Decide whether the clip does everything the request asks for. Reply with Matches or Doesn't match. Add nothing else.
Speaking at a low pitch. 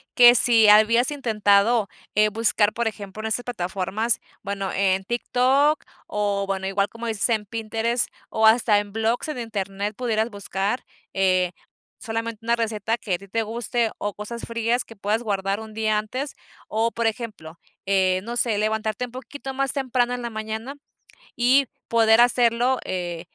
Doesn't match